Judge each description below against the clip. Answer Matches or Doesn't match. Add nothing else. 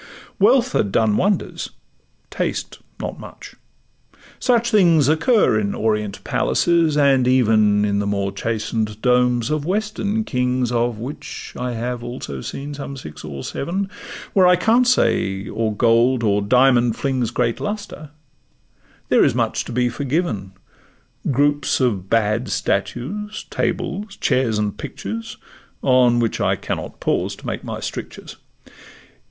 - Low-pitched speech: Matches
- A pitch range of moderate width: Doesn't match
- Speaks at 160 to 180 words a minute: Doesn't match